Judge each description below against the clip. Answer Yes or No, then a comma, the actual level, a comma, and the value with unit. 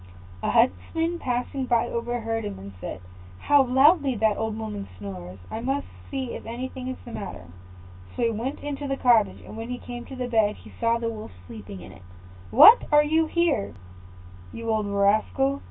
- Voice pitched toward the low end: No, high, 235 Hz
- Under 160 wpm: No, average, 185 wpm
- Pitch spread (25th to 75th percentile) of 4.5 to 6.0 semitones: No, average, 4.1 semitones